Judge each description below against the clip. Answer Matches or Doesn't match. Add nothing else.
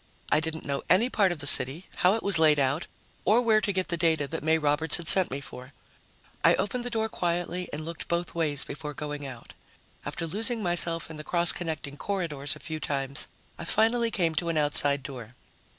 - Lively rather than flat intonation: Doesn't match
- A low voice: Doesn't match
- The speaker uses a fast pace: Matches